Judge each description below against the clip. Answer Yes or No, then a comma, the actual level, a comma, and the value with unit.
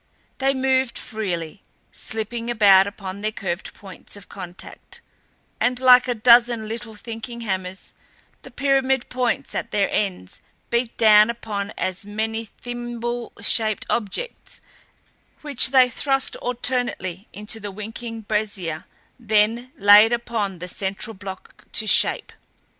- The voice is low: No, high, 220 Hz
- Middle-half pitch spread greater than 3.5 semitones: No, average, 3.2 semitones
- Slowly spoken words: Yes, slow, 125 wpm